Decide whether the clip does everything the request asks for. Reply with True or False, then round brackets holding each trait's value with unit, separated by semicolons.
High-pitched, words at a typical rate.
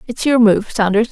False (220 Hz; 215 wpm)